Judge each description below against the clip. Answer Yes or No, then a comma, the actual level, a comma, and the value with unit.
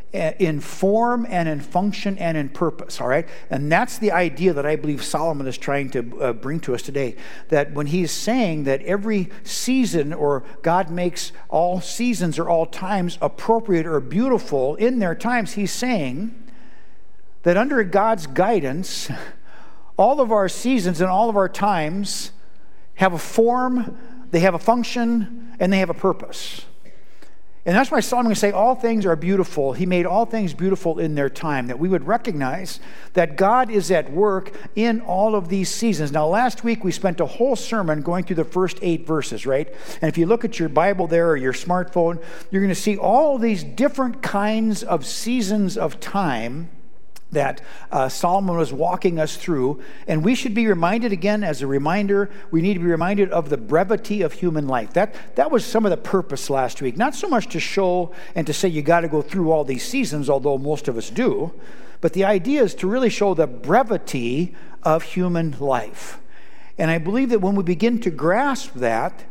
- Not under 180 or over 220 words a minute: Yes, average, 190 wpm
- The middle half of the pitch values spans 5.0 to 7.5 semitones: Yes, wide, 5.4 semitones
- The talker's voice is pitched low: No, medium, 185 Hz